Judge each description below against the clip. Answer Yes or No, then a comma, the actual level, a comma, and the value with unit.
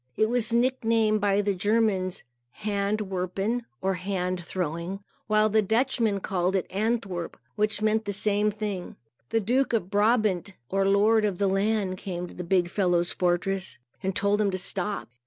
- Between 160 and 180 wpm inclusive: Yes, average, 165 wpm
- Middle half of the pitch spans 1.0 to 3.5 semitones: Yes, narrow, 2.5 semitones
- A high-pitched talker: Yes, high, 200 Hz